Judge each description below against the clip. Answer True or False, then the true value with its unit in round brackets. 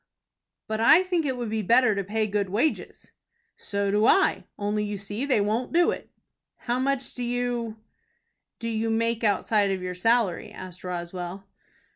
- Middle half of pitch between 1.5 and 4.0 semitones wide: True (3.4 semitones)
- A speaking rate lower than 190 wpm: True (170 wpm)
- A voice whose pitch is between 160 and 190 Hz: False (220 Hz)